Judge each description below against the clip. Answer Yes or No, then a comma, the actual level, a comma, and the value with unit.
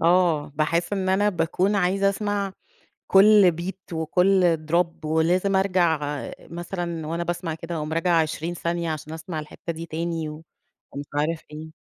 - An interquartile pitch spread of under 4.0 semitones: Yes, narrow, 2.6 semitones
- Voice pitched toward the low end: No, medium, 170 Hz